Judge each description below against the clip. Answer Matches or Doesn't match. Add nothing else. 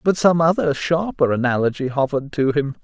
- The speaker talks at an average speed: Matches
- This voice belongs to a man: Matches